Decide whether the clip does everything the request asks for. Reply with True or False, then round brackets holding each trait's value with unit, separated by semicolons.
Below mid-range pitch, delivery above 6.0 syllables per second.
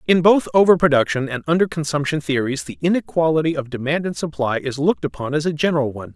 False (150 Hz; 6.6 syllables/s)